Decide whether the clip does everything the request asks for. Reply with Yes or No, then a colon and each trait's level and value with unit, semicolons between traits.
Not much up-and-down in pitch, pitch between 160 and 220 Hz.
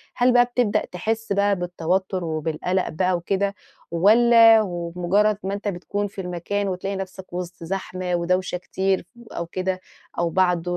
Yes: narrow, 2.3 semitones; medium, 185 Hz